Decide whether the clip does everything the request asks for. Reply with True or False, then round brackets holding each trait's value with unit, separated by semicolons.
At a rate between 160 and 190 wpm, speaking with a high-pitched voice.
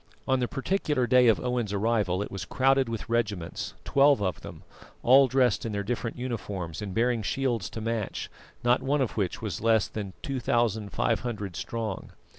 False (170 wpm; 115 Hz)